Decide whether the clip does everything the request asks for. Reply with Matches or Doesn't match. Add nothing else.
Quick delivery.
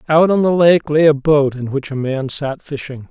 Matches